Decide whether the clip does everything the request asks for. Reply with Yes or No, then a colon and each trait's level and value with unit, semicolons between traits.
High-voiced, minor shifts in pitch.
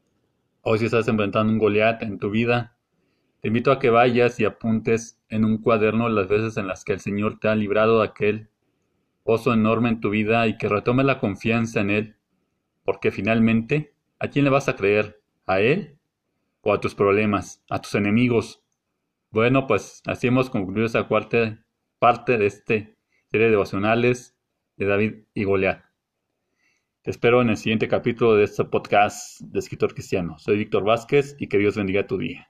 No: low, 110 Hz; narrow, 2.0 semitones